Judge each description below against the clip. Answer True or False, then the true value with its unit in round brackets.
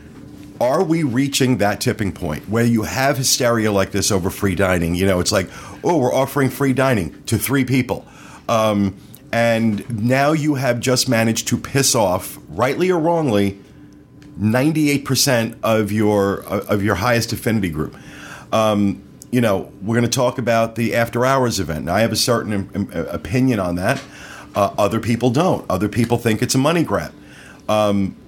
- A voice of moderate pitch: False (115 Hz)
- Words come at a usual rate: True (170 wpm)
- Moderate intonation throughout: True (4.4 semitones)